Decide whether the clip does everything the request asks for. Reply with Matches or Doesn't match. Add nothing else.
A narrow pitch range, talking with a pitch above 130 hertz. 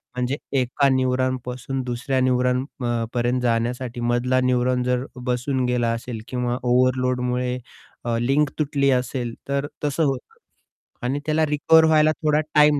Doesn't match